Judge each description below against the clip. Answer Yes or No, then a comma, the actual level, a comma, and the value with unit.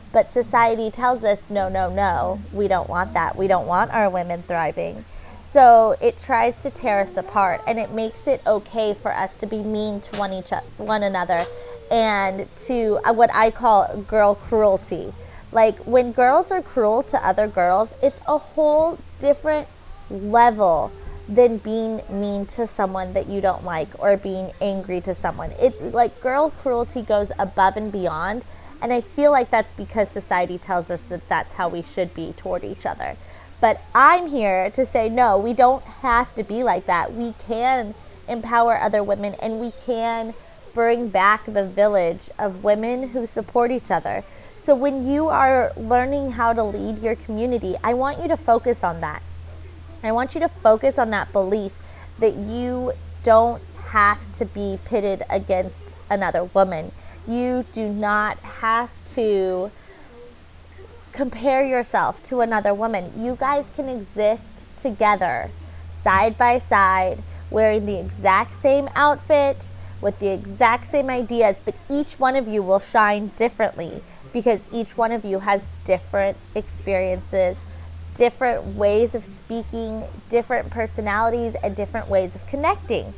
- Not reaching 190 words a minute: Yes, average, 160 wpm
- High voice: Yes, high, 220 Hz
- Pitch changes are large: No, average, 4.0 semitones